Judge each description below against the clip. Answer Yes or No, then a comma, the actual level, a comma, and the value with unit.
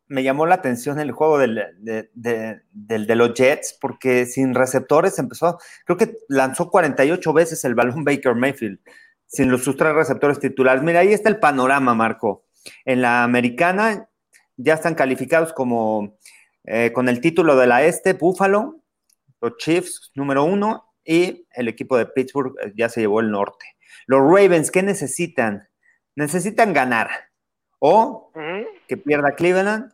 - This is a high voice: No, medium, 140 Hz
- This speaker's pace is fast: No, average, 155 wpm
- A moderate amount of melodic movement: No, wide, 6.2 semitones